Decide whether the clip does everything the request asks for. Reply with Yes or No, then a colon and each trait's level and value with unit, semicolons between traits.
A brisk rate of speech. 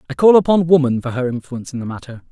Yes: fast, 260 wpm